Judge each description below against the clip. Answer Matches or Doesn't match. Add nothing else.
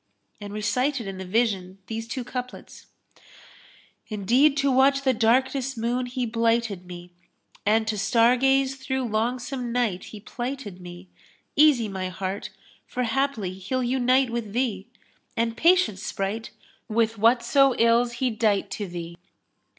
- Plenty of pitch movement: Doesn't match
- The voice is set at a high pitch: Matches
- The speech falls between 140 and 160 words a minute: Matches